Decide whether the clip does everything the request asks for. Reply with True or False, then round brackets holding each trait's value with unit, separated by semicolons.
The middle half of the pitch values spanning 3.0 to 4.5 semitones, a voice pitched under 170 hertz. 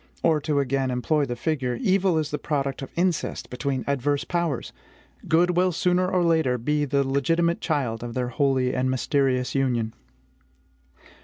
True (4.2 semitones; 140 Hz)